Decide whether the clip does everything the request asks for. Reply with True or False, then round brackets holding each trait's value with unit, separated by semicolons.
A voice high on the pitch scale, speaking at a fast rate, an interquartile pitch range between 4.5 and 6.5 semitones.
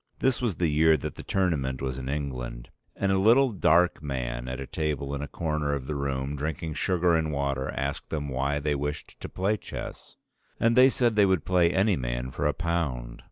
False (75 Hz; 210 wpm; 4.8 semitones)